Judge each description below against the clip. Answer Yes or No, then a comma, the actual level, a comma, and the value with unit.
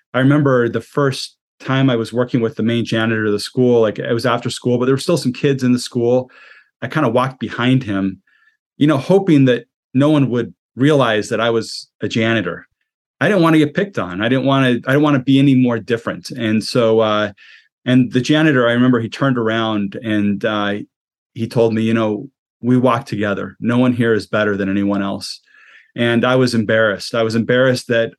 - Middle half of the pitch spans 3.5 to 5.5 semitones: No, average, 2.9 semitones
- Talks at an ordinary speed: No, fast, 220 wpm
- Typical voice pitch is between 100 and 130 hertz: Yes, low, 120 Hz